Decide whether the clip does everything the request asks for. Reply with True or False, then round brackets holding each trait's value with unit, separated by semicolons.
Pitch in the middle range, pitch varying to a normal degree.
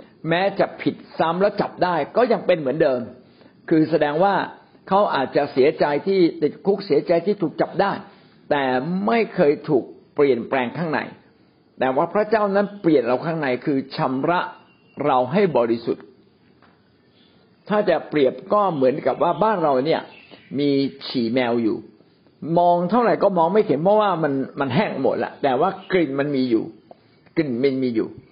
False (165 Hz; 6.3 semitones)